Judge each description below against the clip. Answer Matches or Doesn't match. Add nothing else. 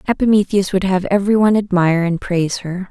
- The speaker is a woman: Matches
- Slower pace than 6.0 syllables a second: Doesn't match